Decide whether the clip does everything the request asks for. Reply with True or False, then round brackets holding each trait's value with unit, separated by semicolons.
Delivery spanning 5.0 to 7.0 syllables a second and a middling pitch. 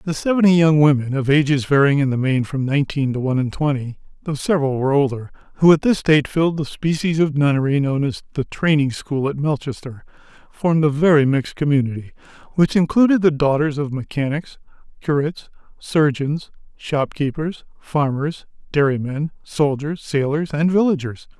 True (5.5 syllables/s; 145 Hz)